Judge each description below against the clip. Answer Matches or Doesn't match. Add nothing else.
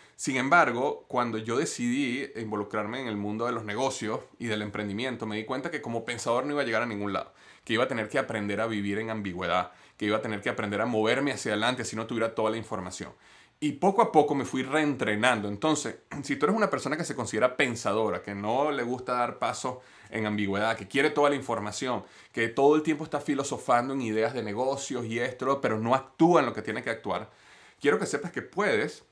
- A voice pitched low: Matches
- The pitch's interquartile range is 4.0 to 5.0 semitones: Matches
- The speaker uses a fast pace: Matches